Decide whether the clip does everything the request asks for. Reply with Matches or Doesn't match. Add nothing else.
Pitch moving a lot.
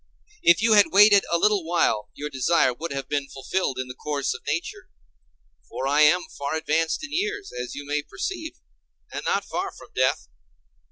Matches